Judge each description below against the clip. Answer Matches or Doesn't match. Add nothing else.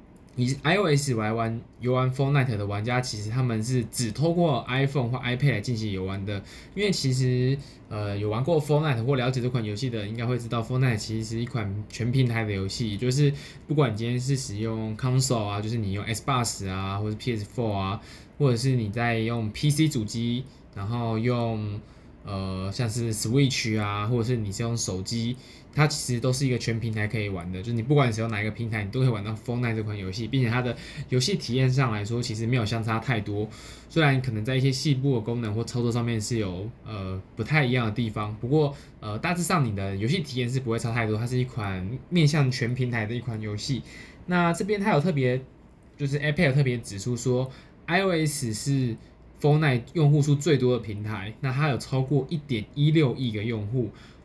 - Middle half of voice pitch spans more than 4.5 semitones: Doesn't match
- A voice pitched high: Doesn't match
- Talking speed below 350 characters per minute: Doesn't match